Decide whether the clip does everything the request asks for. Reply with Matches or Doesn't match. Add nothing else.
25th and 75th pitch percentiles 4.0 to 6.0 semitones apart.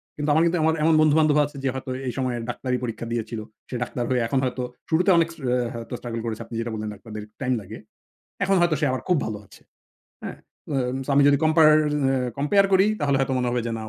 Matches